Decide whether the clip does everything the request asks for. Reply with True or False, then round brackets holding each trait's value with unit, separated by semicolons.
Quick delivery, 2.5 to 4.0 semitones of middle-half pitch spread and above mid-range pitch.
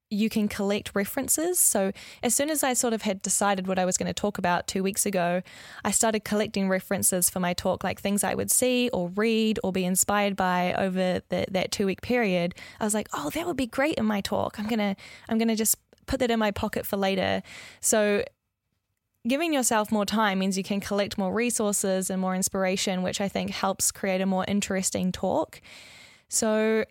True (210 wpm; 2.8 semitones; 200 Hz)